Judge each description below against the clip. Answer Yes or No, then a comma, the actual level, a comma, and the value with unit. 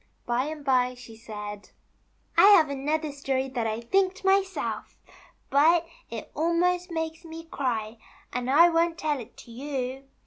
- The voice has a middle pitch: No, very high, 280 Hz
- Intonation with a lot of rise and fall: No, average, 4.9 semitones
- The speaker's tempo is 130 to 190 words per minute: Yes, average, 150 wpm